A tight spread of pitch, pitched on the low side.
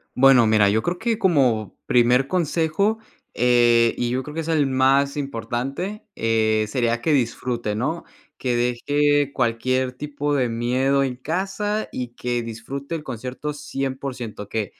No: average, 3.7 semitones; low, 130 Hz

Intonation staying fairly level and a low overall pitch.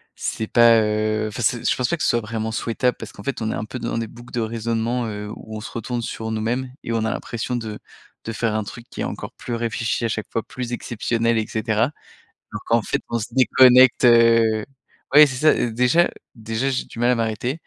Yes: narrow, 1.8 semitones; low, 115 Hz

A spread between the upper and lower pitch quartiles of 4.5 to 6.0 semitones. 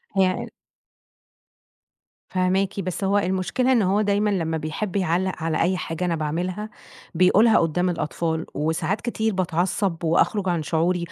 No: average, 3.1 semitones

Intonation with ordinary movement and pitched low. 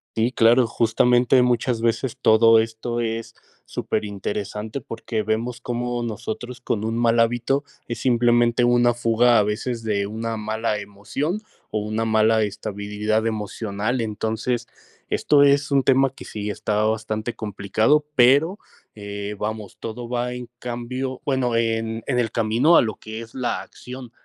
No: narrow, 2.1 semitones; low, 115 Hz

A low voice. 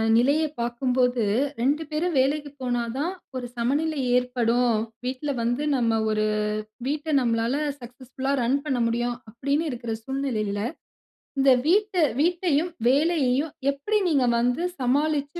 No: very high, 265 Hz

